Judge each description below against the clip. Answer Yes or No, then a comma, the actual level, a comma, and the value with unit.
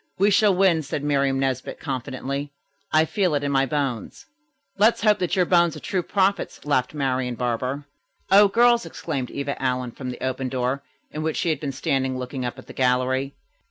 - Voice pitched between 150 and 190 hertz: No, medium, 140 Hz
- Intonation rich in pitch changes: No, average, 4.9 semitones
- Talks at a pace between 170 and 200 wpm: Yes, average, 195 wpm